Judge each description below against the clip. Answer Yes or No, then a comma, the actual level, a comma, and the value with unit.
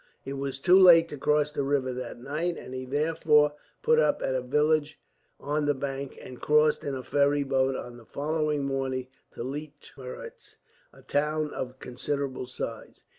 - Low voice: No, medium, 145 Hz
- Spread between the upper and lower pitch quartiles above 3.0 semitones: No, narrow, 2.4 semitones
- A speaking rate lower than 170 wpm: No, average, 175 wpm